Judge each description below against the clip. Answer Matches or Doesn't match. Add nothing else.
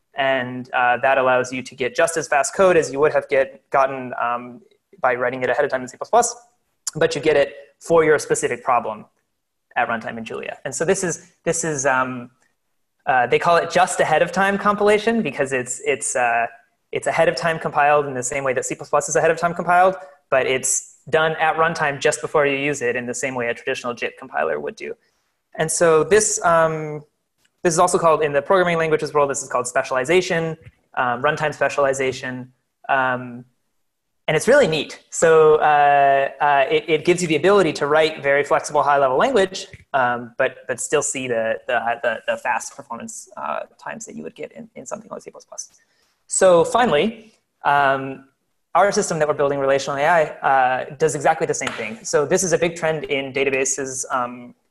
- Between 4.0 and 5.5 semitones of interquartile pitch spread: Matches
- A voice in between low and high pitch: Matches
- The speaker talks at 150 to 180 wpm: Doesn't match